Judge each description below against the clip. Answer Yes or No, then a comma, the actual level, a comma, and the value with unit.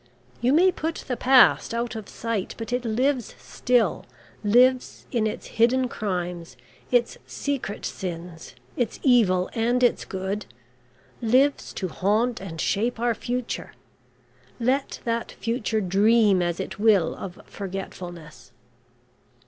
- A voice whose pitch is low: No, high, 225 Hz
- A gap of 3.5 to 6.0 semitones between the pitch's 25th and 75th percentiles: Yes, average, 4.3 semitones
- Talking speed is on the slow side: Yes, slow, 125 wpm